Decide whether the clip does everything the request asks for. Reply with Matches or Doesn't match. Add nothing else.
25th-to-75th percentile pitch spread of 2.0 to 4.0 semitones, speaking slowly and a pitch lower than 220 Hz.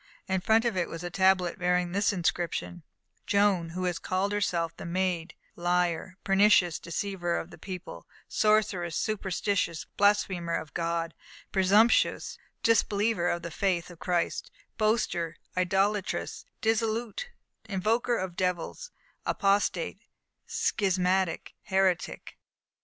Matches